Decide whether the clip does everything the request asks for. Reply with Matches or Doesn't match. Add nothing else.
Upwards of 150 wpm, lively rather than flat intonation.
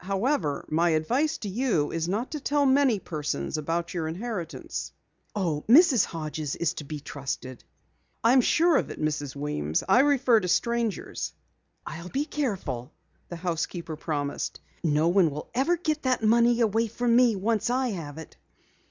Matches